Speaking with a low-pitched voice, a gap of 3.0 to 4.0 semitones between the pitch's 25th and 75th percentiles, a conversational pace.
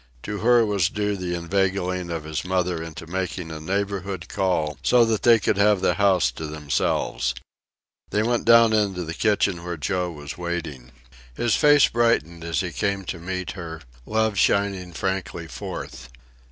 Yes: very low, 90 Hz; average, 3.5 semitones; average, 165 wpm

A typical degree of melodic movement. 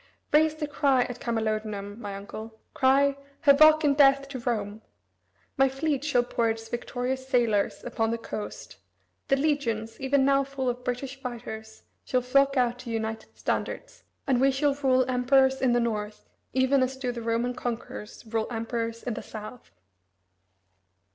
Yes: average, 3.3 semitones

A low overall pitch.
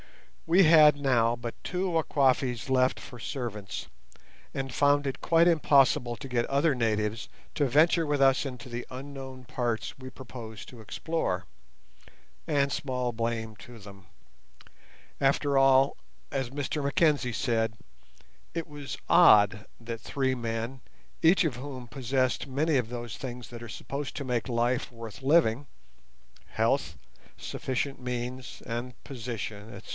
Yes: low, 130 Hz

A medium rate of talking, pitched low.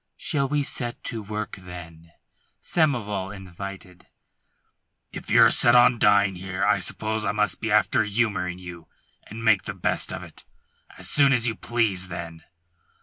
Yes: average, 155 wpm; low, 105 Hz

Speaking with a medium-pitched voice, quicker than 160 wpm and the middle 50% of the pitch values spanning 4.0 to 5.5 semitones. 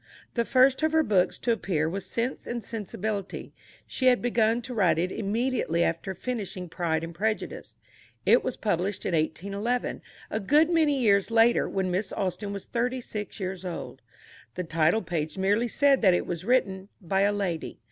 No: high, 200 Hz; average, 180 wpm; average, 4.7 semitones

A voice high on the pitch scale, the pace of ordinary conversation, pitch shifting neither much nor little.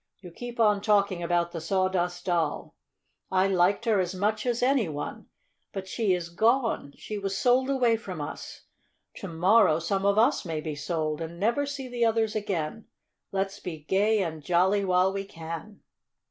Yes: high, 195 Hz; average, 175 wpm; average, 4.2 semitones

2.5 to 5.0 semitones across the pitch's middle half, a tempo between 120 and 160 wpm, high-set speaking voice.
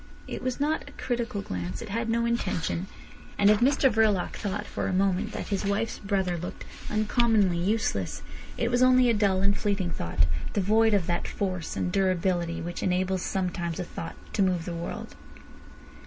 No: average, 3.8 semitones; average, 180 wpm; high, 195 Hz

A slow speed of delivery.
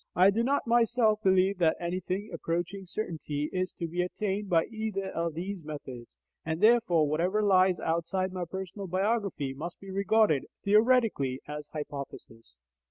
No: average, 150 wpm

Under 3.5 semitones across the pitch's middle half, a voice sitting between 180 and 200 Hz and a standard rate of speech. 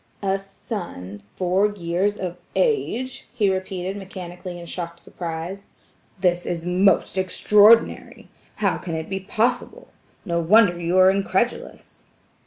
No: average, 2.7 semitones; high, 190 Hz; slow, 125 wpm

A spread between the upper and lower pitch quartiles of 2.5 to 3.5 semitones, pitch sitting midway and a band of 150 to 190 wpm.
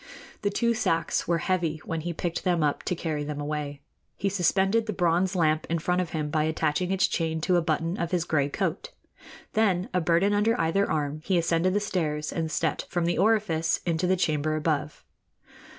No: average, 3.0 semitones; medium, 170 Hz; average, 200 wpm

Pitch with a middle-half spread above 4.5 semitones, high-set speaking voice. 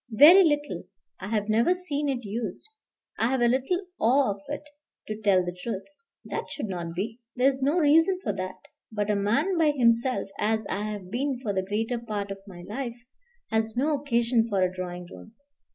Yes: average, 5.3 semitones; high, 230 Hz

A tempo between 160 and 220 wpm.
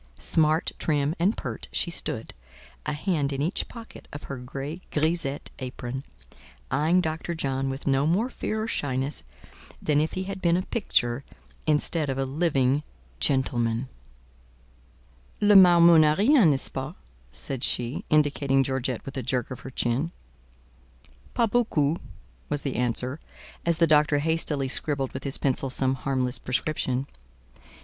No: average, 150 wpm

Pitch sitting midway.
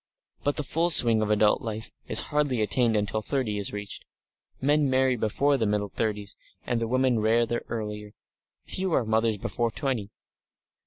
No: low, 115 Hz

